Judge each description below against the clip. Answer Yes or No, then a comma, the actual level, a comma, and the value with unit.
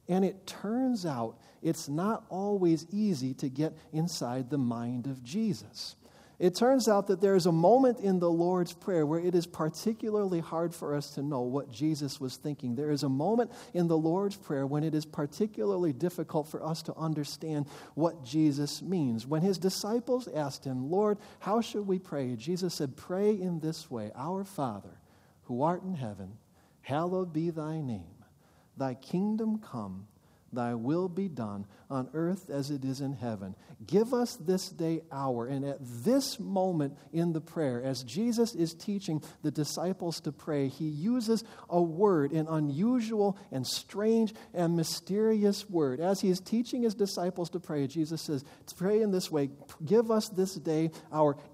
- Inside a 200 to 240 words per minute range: No, average, 175 wpm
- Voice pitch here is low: No, medium, 165 Hz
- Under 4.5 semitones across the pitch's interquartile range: No, average, 5.2 semitones